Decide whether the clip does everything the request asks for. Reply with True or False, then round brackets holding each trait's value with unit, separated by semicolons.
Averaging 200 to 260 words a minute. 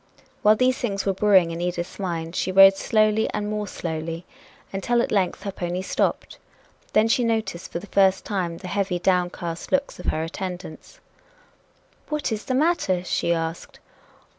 False (165 wpm)